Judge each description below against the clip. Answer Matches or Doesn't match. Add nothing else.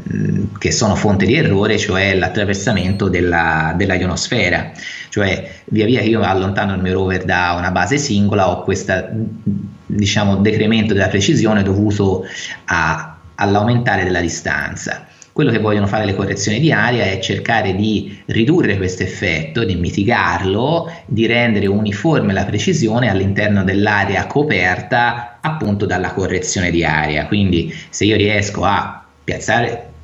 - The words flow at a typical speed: Matches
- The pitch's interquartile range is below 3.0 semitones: Matches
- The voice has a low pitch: Matches